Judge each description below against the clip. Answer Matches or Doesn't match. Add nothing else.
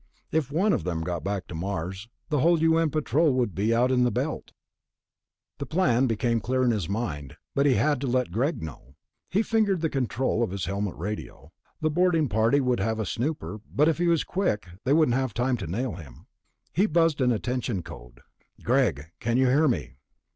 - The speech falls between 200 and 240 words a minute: Matches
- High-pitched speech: Doesn't match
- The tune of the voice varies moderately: Doesn't match